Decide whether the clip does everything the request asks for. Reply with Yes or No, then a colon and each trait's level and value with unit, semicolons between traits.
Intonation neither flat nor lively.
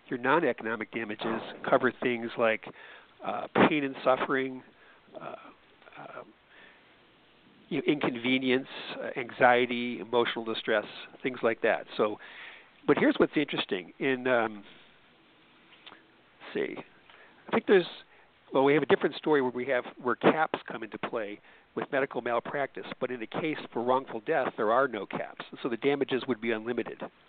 No: narrow, 2.2 semitones